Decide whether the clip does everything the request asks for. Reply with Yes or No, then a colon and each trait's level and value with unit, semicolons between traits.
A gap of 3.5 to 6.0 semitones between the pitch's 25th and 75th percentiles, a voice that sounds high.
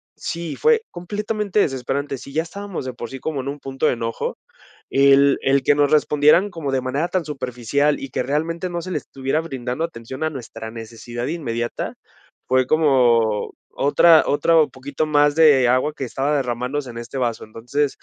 No: average, 3.9 semitones; medium, 140 Hz